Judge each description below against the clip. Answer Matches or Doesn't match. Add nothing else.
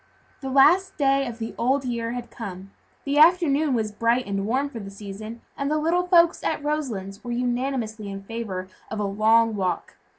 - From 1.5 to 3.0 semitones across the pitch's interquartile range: Doesn't match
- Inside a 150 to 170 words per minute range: Doesn't match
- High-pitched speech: Matches